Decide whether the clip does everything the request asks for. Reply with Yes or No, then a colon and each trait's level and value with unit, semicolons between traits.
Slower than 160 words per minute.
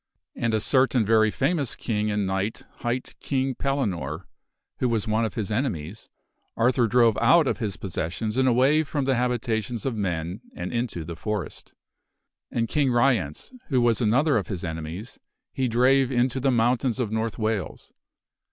No: average, 170 wpm